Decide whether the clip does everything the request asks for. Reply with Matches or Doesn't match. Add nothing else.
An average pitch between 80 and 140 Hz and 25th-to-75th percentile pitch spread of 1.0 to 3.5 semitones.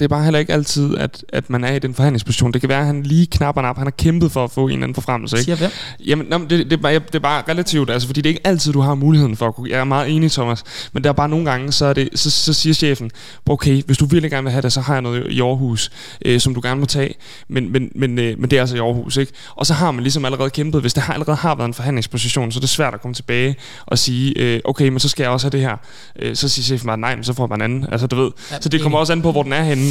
Matches